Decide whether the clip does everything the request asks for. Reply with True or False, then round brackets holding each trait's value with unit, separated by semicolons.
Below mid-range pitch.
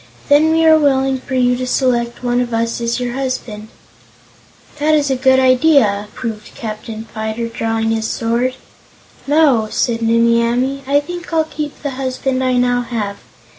False (250 Hz)